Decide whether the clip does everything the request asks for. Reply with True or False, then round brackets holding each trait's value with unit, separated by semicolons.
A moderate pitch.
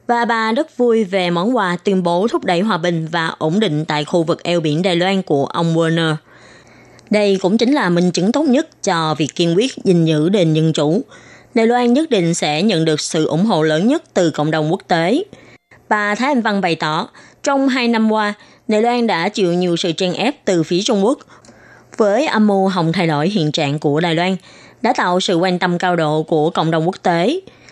True (180 Hz)